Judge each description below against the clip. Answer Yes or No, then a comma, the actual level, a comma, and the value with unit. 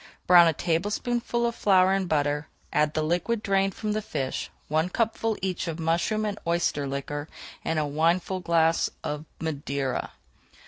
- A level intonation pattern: No, average, 4.5 semitones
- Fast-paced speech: No, average, 150 wpm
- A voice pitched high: No, medium, 170 Hz